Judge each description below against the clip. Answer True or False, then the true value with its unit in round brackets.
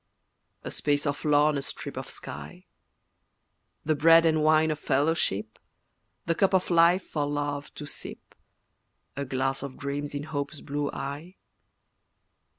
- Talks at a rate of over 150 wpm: False (145 wpm)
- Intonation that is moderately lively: False (1.9 semitones)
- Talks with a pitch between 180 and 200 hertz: False (145 Hz)